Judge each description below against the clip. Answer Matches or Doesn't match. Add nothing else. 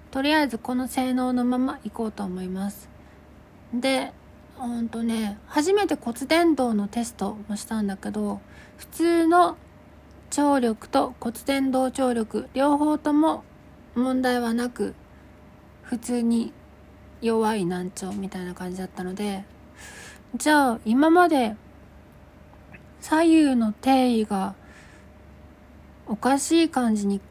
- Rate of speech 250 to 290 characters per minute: Doesn't match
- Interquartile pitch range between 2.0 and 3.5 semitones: Doesn't match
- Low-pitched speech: Doesn't match